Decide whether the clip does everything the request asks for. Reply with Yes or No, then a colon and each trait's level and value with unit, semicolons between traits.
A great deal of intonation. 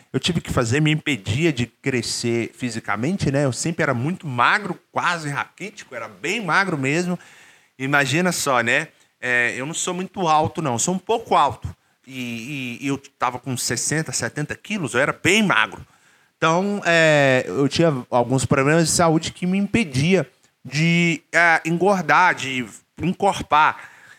No: average, 4.9 semitones